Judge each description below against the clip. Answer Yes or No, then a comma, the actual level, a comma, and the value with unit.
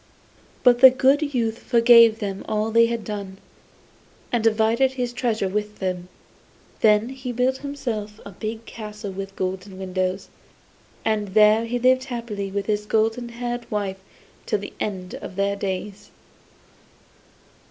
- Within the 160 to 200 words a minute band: No, average, 140 wpm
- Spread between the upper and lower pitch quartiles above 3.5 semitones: No, average, 3.1 semitones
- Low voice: No, high, 215 Hz